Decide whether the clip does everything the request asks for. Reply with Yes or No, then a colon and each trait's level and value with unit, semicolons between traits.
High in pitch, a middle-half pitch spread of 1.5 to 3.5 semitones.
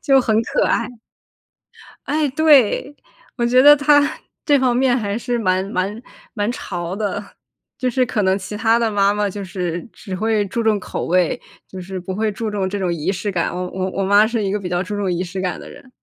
No: high, 205 Hz; average, 4.1 semitones